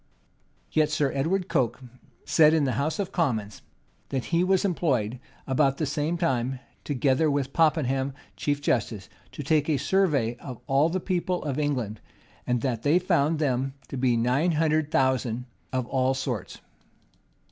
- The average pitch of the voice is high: No, medium, 140 Hz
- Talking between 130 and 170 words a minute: Yes, average, 160 wpm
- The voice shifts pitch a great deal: No, average, 3.7 semitones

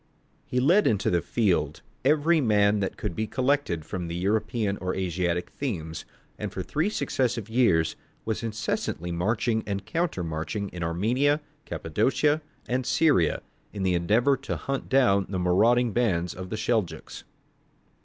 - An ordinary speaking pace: Yes, average, 150 wpm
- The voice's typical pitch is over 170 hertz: No, low, 105 Hz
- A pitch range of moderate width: No, wide, 6.0 semitones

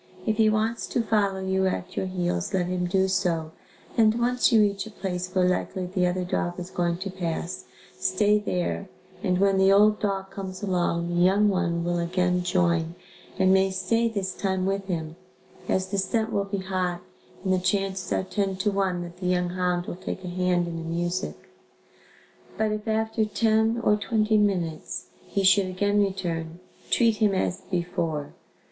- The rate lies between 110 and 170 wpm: No, average, 185 wpm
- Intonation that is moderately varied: No, narrow, 2.3 semitones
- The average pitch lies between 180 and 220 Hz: Yes, high, 190 Hz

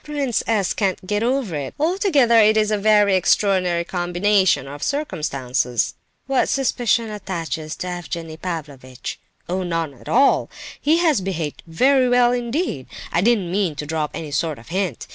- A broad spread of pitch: Yes, wide, 6.7 semitones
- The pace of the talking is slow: No, average, 160 wpm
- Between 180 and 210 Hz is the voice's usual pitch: Yes, high, 190 Hz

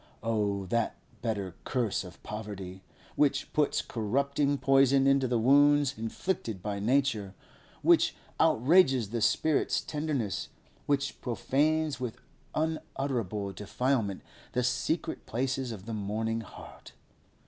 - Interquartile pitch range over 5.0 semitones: No, average, 4.7 semitones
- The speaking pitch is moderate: No, low, 125 Hz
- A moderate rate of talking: No, slow, 115 wpm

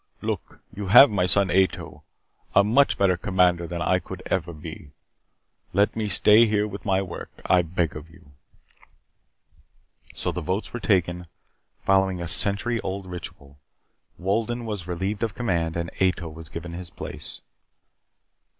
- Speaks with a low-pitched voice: Yes, very low, 95 Hz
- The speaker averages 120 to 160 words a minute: Yes, average, 150 wpm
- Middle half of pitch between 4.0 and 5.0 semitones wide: No, average, 2.9 semitones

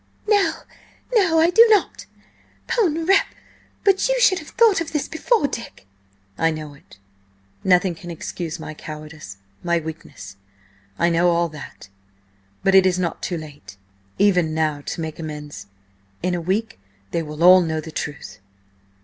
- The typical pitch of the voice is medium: Yes, medium, 170 Hz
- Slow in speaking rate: No, average, 155 wpm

